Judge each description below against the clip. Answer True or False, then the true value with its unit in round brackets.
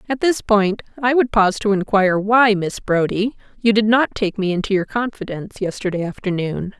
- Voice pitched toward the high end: True (205 Hz)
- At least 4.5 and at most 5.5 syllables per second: True (5.4 syllables/s)